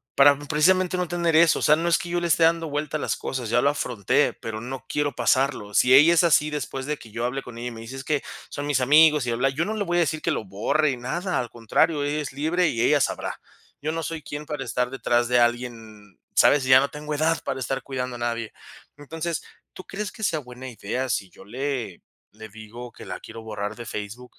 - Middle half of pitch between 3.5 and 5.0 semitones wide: Yes, average, 4.5 semitones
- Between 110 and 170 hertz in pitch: Yes, low, 135 Hz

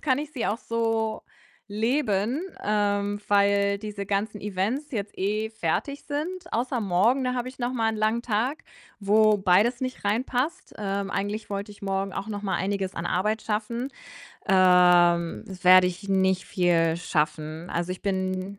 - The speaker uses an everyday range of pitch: Yes, average, 3.3 semitones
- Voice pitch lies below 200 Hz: No, high, 205 Hz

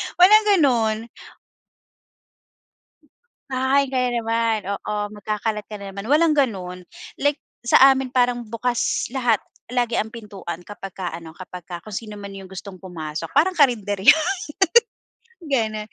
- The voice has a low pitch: No, high, 220 Hz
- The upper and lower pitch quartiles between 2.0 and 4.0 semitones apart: No, average, 4.7 semitones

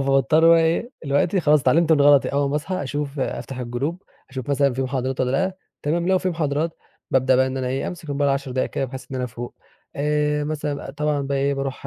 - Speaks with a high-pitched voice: No, medium, 140 Hz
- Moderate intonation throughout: No, narrow, 2.3 semitones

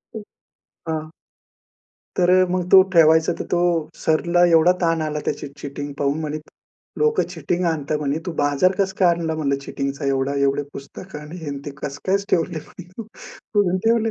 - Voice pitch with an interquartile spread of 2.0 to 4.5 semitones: Yes, average, 3.9 semitones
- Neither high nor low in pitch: Yes, medium, 160 Hz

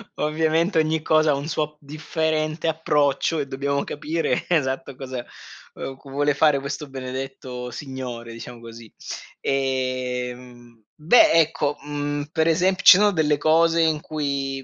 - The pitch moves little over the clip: No, average, 3.1 semitones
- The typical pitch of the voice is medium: Yes, medium, 145 Hz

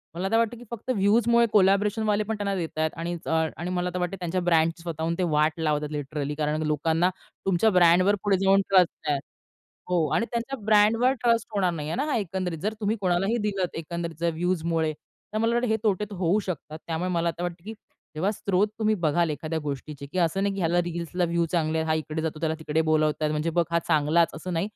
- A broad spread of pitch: No, average, 3.9 semitones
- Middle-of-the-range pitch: Yes, medium, 175 Hz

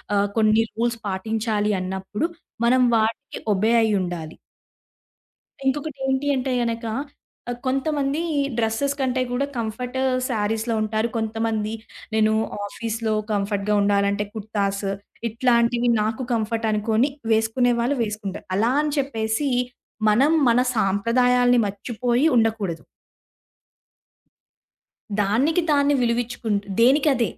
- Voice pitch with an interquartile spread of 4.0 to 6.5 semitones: No, average, 2.9 semitones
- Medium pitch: No, high, 225 Hz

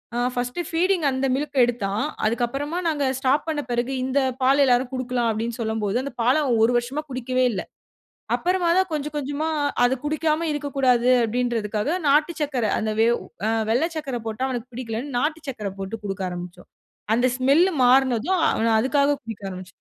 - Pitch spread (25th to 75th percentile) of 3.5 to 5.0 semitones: Yes, average, 4.1 semitones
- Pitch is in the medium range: No, very high, 255 Hz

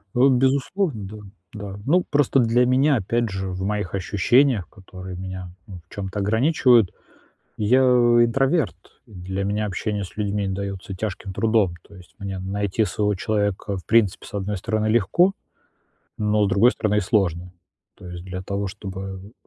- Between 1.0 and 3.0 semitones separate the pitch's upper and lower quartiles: No, average, 3.5 semitones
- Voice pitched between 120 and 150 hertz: No, low, 105 Hz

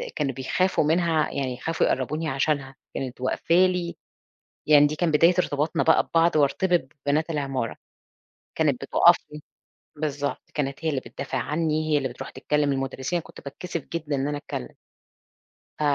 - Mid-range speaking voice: Yes, medium, 150 Hz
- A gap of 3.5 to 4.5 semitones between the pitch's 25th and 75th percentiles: No, average, 3.1 semitones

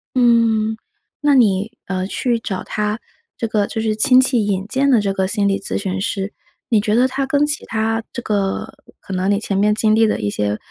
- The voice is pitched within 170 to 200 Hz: No, high, 215 Hz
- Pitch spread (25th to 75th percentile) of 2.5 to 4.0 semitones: Yes, average, 2.9 semitones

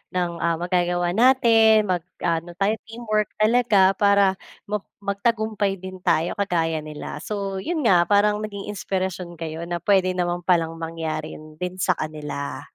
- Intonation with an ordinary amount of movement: Yes, average, 3.5 semitones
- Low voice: No, medium, 185 Hz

